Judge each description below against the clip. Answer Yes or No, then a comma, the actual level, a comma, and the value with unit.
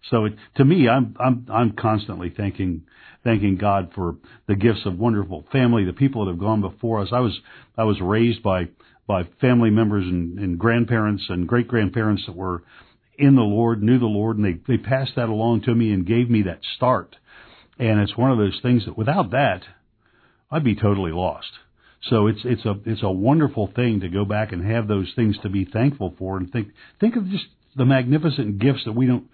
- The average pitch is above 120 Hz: No, low, 110 Hz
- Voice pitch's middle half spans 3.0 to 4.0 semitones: Yes, average, 3.4 semitones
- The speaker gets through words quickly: Yes, fast, 210 wpm